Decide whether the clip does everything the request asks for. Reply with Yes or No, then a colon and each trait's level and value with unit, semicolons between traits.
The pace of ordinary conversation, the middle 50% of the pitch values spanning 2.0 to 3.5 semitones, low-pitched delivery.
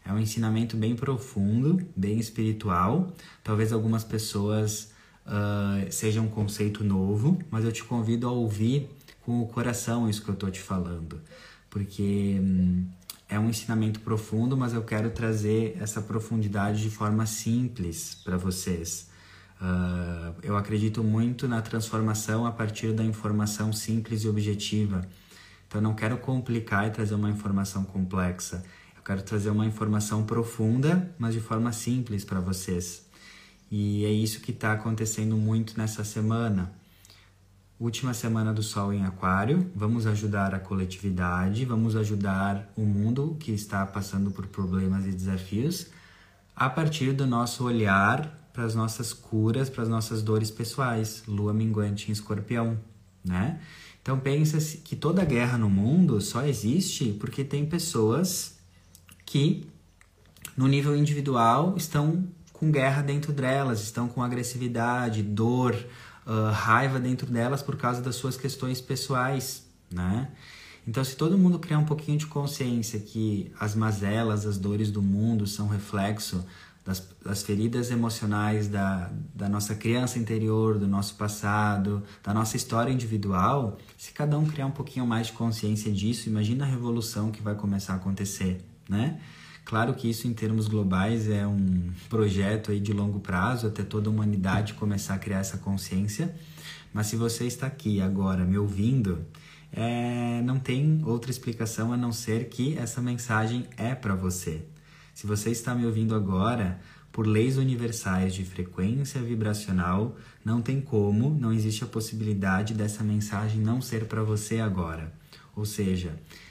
Yes: average, 150 wpm; average, 3.2 semitones; low, 110 Hz